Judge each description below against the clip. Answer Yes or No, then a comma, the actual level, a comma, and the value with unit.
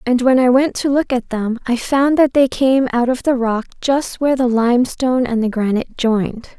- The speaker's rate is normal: No, fast, 230 wpm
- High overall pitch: Yes, very high, 250 Hz